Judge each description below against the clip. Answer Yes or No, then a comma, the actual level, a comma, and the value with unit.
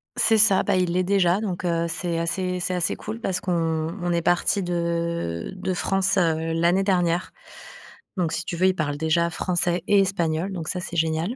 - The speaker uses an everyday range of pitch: No, narrow, 2.0 semitones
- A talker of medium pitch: Yes, medium, 175 Hz